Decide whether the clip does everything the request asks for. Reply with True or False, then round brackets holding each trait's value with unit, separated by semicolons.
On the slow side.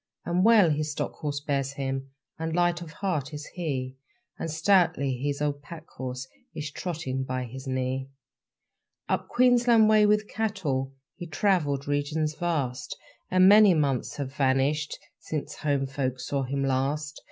False (155 wpm)